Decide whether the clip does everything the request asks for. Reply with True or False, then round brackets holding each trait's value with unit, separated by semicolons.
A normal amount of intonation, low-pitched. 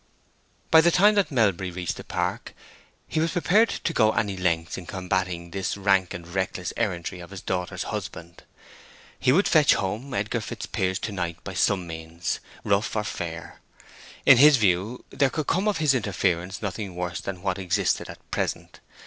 False (6.0 semitones; 95 Hz)